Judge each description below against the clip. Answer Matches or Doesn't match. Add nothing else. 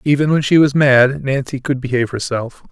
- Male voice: Matches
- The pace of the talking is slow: Doesn't match